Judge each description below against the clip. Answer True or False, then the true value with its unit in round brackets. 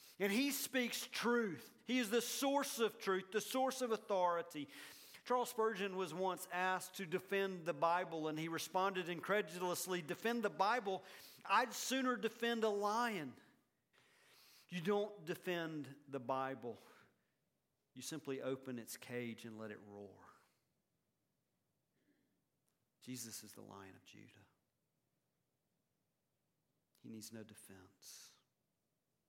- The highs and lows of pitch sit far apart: True (8.5 semitones)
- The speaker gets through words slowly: True (120 wpm)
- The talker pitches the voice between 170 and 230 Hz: True (185 Hz)